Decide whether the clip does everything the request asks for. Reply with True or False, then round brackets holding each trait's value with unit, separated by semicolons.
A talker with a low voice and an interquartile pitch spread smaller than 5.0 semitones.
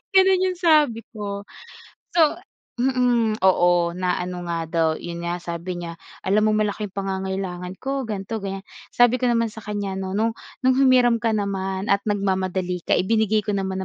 False (200 Hz; 3.6 semitones)